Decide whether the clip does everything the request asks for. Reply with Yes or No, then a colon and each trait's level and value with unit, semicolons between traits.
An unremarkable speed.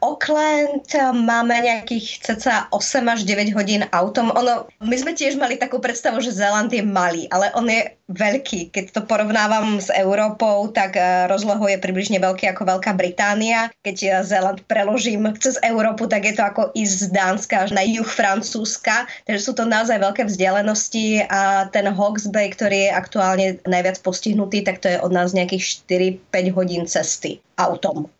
No: fast, 170 wpm